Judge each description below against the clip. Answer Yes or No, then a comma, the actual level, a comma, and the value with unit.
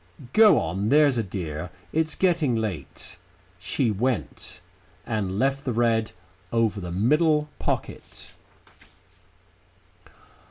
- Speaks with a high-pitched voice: No, low, 115 Hz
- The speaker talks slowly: Yes, slow, 105 wpm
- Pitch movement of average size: No, wide, 6.8 semitones